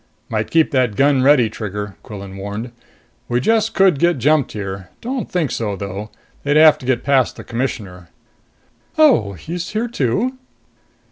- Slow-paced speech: No, average, 155 wpm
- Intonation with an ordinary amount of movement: No, wide, 7.9 semitones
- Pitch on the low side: Yes, low, 130 Hz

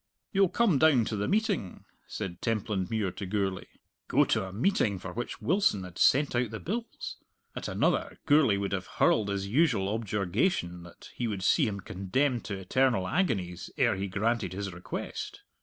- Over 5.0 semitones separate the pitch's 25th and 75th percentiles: Yes, wide, 5.6 semitones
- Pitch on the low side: Yes, low, 105 Hz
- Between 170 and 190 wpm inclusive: Yes, average, 175 wpm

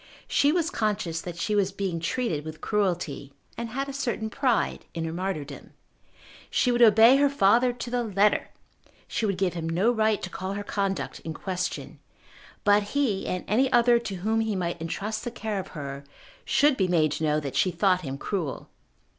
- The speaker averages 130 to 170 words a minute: No, average, 195 wpm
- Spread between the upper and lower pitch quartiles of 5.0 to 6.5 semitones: Yes, average, 5.3 semitones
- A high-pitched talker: Yes, high, 200 Hz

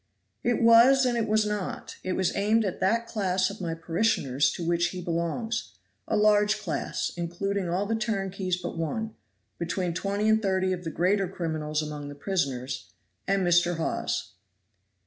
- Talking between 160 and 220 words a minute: Yes, average, 165 wpm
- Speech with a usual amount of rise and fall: Yes, average, 3.9 semitones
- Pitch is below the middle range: No, medium, 185 Hz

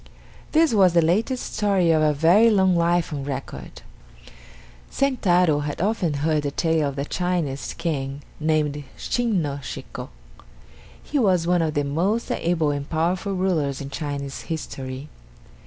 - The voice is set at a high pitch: No, medium, 165 Hz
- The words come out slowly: No, average, 150 wpm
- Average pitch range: Yes, average, 4.2 semitones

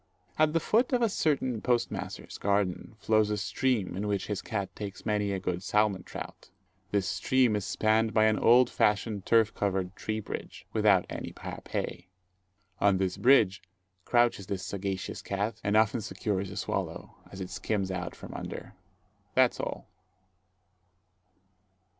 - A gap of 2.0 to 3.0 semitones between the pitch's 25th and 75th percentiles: Yes, average, 2.7 semitones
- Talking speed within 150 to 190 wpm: Yes, average, 155 wpm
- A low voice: Yes, low, 105 Hz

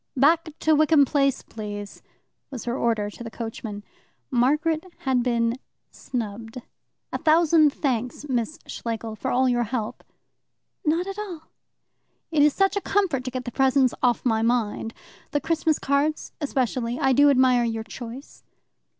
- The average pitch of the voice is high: Yes, very high, 255 Hz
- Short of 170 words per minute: Yes, average, 150 wpm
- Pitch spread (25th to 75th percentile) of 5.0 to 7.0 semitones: No, average, 4.5 semitones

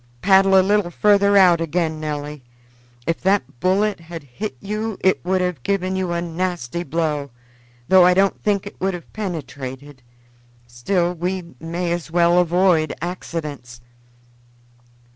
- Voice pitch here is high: No, medium, 175 Hz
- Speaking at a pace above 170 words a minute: No, average, 140 wpm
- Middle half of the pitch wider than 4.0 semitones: No, average, 3.2 semitones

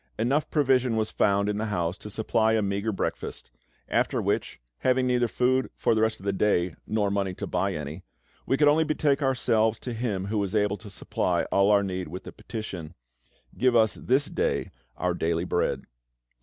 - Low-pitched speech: Yes, low, 110 Hz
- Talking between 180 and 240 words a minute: Yes, average, 195 wpm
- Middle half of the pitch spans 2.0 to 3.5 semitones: No, average, 4.0 semitones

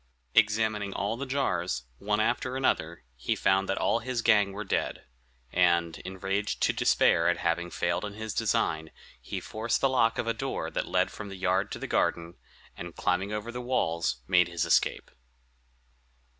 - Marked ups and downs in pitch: No, average, 4.2 semitones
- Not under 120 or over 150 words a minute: No, average, 175 wpm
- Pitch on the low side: Yes, low, 100 Hz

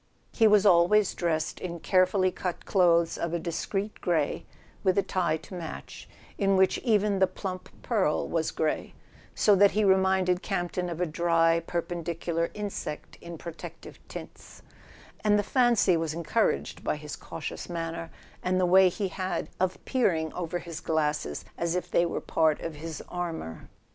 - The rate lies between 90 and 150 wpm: No, average, 165 wpm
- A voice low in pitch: No, medium, 175 Hz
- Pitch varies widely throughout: No, narrow, 2.5 semitones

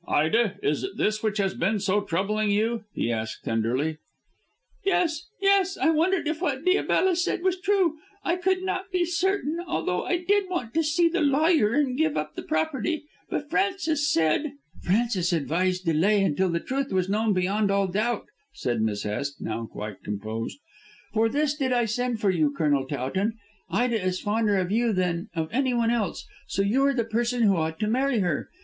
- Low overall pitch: No, high, 225 Hz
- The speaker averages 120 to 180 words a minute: No, average, 190 wpm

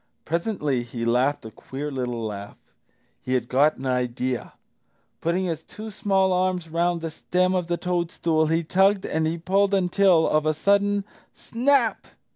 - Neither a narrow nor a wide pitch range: No, wide, 5.8 semitones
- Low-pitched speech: No, medium, 165 Hz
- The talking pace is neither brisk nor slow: Yes, average, 160 wpm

